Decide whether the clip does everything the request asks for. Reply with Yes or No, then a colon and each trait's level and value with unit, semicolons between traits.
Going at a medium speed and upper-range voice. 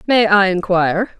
Yes: average, 150 wpm; high, 195 Hz